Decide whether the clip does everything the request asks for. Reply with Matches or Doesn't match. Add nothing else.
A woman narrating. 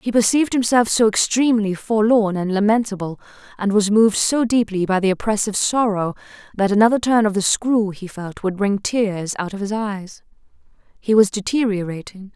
Matches